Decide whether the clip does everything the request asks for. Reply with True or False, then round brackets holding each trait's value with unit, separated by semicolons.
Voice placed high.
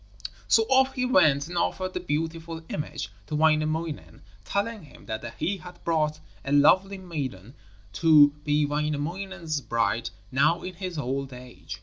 False (155 Hz)